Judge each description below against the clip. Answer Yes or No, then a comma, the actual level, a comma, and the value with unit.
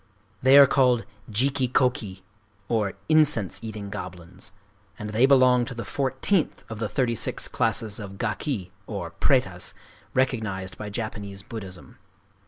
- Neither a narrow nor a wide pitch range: Yes, average, 4.5 semitones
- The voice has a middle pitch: No, low, 115 Hz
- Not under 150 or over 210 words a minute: No, slow, 135 wpm